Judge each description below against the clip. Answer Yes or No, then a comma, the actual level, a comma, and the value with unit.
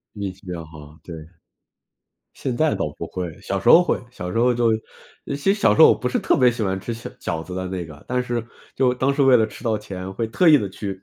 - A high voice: No, low, 110 Hz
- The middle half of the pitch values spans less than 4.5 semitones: No, wide, 5.4 semitones